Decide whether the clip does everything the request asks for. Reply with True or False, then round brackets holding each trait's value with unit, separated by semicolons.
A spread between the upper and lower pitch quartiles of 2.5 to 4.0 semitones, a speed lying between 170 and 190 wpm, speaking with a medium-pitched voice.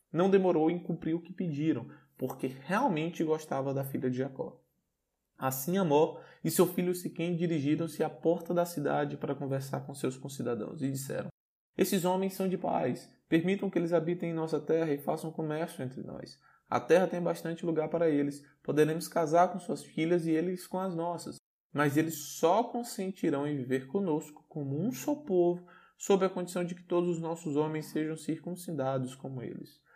True (3.1 semitones; 180 wpm; 165 Hz)